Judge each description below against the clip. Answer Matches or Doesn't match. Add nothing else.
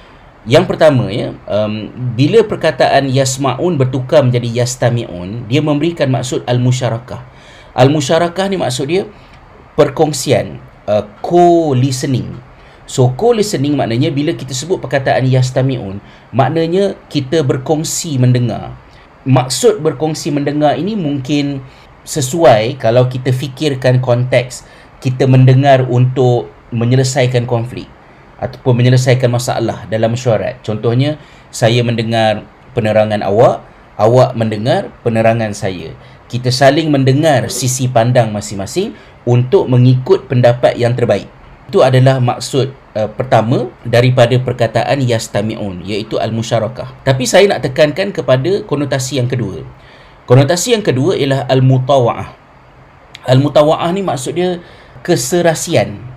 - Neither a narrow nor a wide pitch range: Matches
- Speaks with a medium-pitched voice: Doesn't match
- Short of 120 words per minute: Matches